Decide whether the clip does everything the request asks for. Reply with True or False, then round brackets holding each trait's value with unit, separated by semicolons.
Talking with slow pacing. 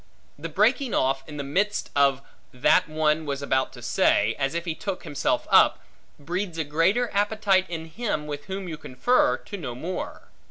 False (185 wpm)